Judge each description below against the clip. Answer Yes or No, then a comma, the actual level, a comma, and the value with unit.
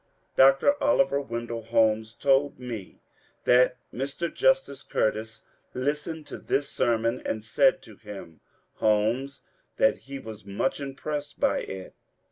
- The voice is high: No, low, 125 Hz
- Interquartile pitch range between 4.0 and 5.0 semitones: Yes, average, 4.4 semitones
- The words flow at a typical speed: No, slow, 130 wpm